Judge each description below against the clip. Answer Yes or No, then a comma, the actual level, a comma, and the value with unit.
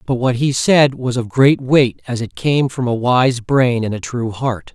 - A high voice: No, low, 125 Hz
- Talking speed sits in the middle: No, fast, 240 wpm